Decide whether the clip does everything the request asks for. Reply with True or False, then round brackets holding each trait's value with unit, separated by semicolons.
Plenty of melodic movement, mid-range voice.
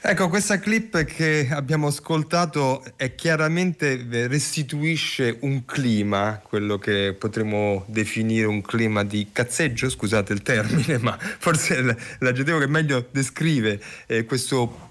False (6.1 semitones; 130 Hz)